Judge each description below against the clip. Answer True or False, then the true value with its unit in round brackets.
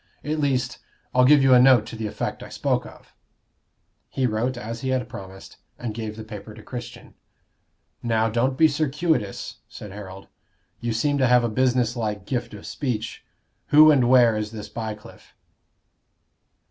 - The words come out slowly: False (170 wpm)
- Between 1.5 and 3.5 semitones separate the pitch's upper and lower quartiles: True (3.2 semitones)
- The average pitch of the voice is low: True (120 Hz)